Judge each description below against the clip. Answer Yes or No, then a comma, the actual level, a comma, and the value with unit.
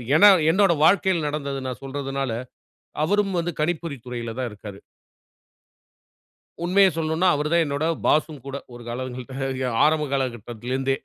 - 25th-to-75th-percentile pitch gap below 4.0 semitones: No, average, 4.4 semitones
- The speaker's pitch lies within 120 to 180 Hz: Yes, medium, 140 Hz